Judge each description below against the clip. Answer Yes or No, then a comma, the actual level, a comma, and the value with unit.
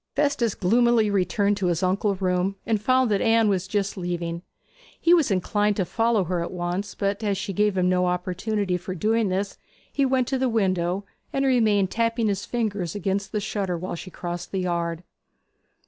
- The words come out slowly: No, average, 190 wpm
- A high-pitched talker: Yes, high, 200 Hz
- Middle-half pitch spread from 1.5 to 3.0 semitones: No, average, 3.4 semitones